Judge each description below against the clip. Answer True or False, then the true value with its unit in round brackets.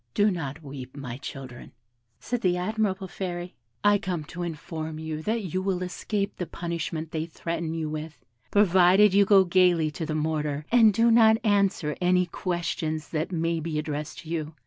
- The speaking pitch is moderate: True (170 Hz)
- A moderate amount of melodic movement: True (3.5 semitones)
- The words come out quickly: False (175 wpm)